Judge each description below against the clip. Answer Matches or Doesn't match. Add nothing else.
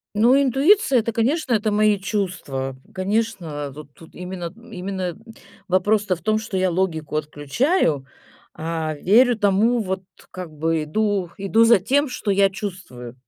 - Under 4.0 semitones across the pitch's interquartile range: Doesn't match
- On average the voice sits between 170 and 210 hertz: Matches